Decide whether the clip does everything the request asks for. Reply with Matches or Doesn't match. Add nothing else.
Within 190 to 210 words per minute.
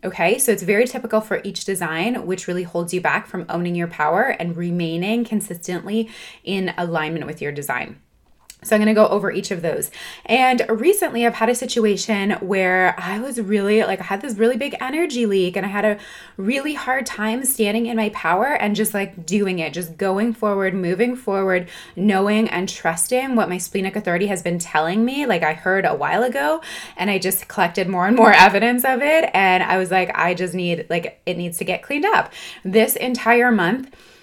Matches